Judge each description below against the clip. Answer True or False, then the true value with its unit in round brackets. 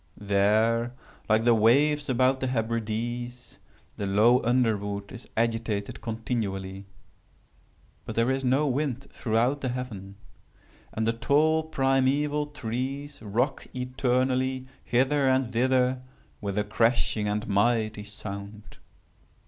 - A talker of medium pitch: False (120 Hz)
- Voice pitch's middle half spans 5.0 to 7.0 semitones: False (3.3 semitones)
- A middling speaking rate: False (115 wpm)